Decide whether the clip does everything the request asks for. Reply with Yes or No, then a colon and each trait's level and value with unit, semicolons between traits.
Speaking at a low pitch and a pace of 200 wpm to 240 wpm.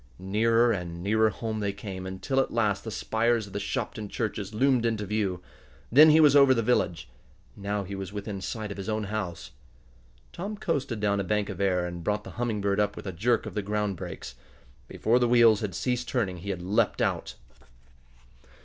Yes: low, 105 Hz; fast, 205 wpm